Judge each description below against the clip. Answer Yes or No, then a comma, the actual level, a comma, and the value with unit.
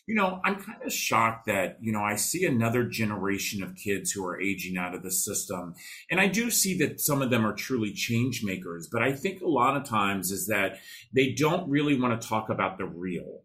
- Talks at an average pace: No, fast, 230 wpm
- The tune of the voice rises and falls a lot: Yes, wide, 6.4 semitones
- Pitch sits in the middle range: No, low, 115 Hz